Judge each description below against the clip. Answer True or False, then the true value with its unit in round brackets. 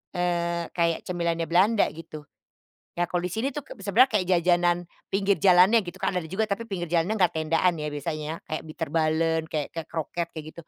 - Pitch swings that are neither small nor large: False (2.2 semitones)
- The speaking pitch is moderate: True (175 Hz)